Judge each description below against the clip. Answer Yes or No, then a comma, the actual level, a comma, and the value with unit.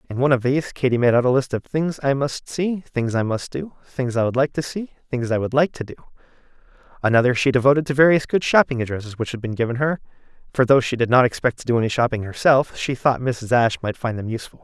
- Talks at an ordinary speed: No, fast, 255 wpm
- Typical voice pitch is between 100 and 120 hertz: No, low, 130 Hz